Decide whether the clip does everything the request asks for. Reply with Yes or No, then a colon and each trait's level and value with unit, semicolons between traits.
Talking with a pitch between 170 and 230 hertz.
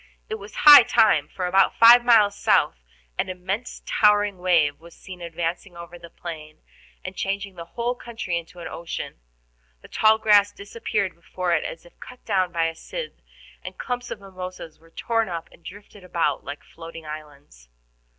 Yes: medium, 185 Hz